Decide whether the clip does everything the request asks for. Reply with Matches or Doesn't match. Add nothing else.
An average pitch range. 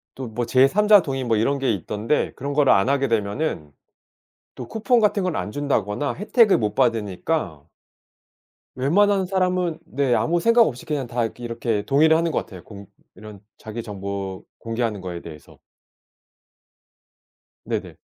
Doesn't match